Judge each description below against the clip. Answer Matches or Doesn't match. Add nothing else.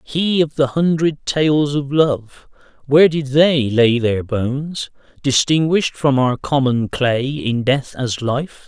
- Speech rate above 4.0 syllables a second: Doesn't match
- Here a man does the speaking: Matches